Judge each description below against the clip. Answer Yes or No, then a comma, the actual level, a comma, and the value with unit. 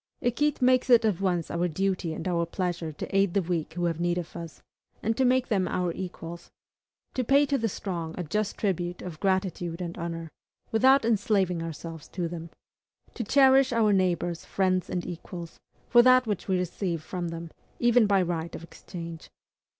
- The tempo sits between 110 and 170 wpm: No, average, 185 wpm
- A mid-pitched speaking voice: Yes, medium, 180 Hz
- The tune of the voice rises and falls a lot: No, average, 4.4 semitones